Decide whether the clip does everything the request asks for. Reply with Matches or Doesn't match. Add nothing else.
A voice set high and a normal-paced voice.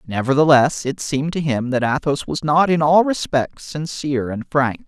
Doesn't match